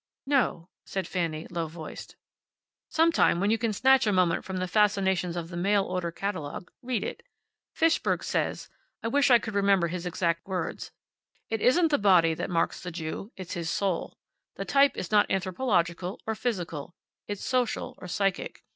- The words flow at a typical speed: Yes, average, 175 wpm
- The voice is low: No, high, 190 Hz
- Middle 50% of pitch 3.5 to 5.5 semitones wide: Yes, average, 4.3 semitones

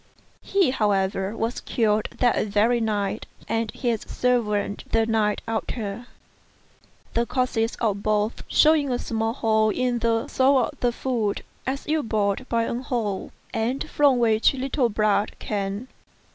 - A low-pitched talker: No, high, 225 Hz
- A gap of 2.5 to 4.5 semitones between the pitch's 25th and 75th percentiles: Yes, average, 2.9 semitones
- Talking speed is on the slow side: No, average, 145 wpm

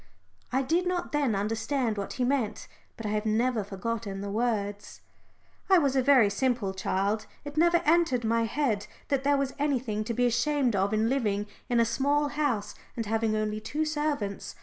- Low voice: No, high, 235 Hz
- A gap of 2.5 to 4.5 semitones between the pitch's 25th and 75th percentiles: No, average, 4.9 semitones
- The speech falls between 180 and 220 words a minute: Yes, average, 185 wpm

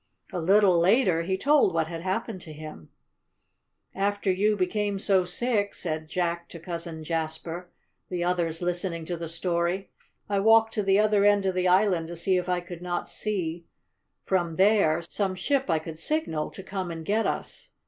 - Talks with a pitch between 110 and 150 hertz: No, medium, 180 Hz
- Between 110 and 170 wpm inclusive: No, average, 180 wpm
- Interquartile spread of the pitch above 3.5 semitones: No, average, 3.1 semitones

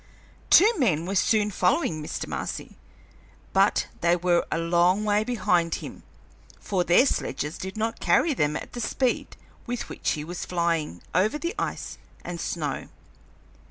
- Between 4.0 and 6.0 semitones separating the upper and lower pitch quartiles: Yes, average, 4.4 semitones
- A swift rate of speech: No, average, 155 wpm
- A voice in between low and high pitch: Yes, medium, 180 Hz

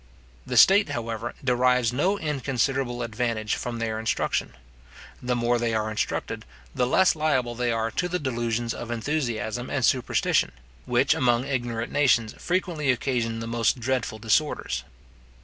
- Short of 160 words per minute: Yes, average, 145 wpm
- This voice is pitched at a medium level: No, low, 120 Hz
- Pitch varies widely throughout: No, average, 2.7 semitones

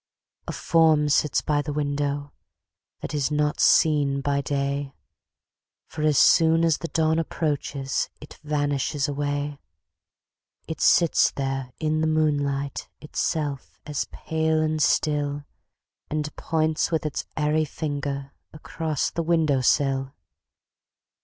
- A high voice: No, medium, 150 Hz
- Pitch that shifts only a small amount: Yes, narrow, 1.7 semitones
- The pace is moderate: No, slow, 120 wpm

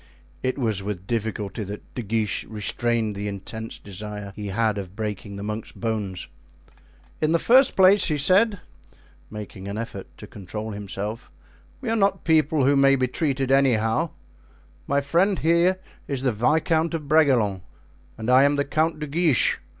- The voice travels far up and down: Yes, wide, 6.8 semitones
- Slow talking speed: No, average, 165 wpm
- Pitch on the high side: No, low, 120 Hz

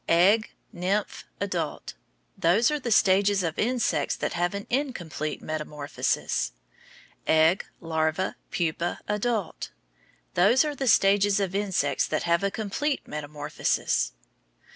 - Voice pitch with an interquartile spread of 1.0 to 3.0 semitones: No, average, 4.8 semitones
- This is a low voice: No, high, 190 Hz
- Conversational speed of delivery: No, slow, 120 wpm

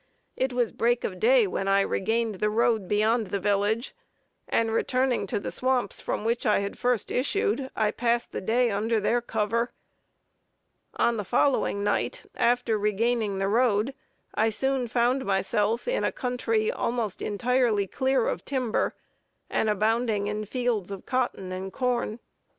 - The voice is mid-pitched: No, high, 230 Hz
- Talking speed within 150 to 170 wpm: Yes, average, 155 wpm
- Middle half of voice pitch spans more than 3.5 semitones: No, average, 3.0 semitones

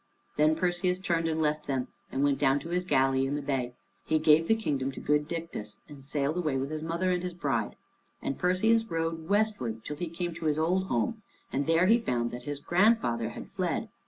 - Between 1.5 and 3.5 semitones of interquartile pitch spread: No, average, 4.5 semitones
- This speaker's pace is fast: Yes, fast, 215 wpm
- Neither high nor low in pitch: Yes, medium, 155 Hz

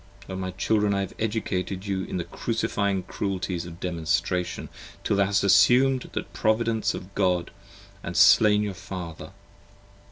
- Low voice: Yes, very low, 95 Hz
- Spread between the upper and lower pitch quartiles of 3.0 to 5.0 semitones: No, narrow, 2.4 semitones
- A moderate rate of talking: Yes, average, 155 wpm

